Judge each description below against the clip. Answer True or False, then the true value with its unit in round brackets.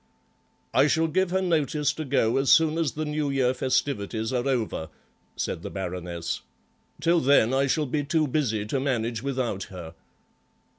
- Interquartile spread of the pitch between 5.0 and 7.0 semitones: True (5.4 semitones)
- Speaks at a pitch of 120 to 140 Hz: True (135 Hz)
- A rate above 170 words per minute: False (165 wpm)